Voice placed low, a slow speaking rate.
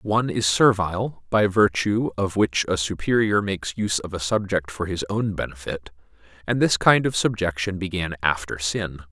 No: very low, 95 Hz; average, 170 wpm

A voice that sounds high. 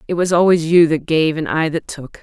No: medium, 160 Hz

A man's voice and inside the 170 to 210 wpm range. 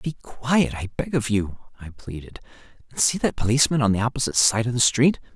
Yes: male; average, 200 wpm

